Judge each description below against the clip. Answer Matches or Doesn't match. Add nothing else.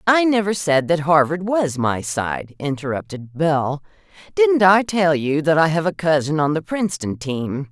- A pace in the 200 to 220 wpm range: Doesn't match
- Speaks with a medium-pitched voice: Matches